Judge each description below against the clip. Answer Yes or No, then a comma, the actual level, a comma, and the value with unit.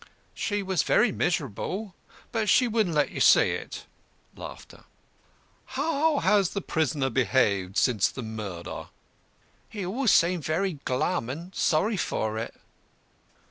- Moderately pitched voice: Yes, medium, 170 Hz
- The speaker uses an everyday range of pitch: No, wide, 8.3 semitones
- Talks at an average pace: No, slow, 130 wpm